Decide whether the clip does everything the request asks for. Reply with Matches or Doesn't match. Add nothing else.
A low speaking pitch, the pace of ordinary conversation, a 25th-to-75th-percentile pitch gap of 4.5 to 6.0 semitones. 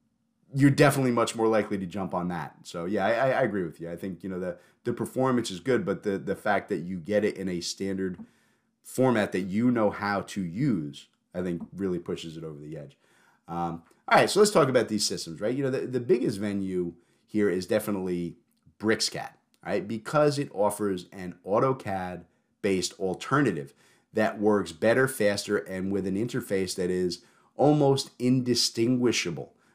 Matches